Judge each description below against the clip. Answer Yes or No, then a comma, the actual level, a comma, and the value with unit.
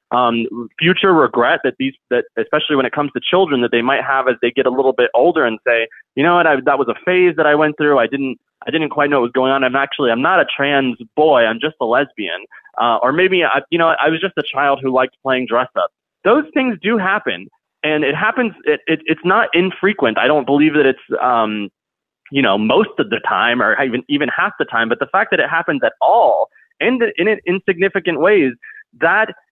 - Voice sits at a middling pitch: Yes, medium, 150 Hz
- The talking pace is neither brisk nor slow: No, fast, 240 wpm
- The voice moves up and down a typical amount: No, wide, 5.9 semitones